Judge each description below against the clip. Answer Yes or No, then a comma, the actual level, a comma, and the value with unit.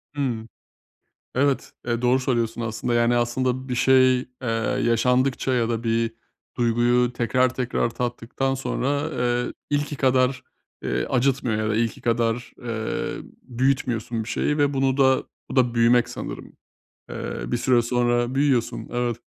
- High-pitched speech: No, low, 125 Hz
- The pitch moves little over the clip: Yes, narrow, 1.8 semitones